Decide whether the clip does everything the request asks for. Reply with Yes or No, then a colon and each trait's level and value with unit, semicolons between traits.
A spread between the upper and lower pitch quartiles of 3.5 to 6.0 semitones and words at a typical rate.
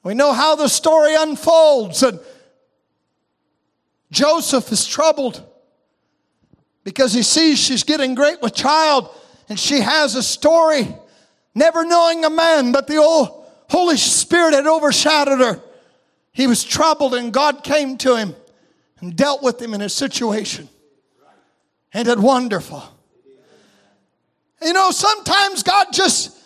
No: average, 3.9 semitones; slow, 130 wpm